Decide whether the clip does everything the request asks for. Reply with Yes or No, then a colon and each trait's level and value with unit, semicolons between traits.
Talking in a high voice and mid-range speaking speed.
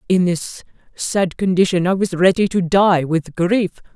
No: medium, 180 Hz; average, 165 wpm